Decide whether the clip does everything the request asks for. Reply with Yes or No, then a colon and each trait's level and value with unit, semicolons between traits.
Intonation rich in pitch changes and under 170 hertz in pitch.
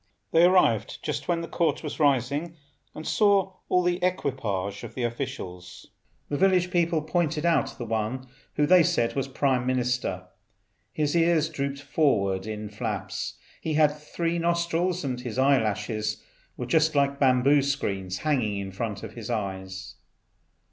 Yes: wide, 6.9 semitones; medium, 140 Hz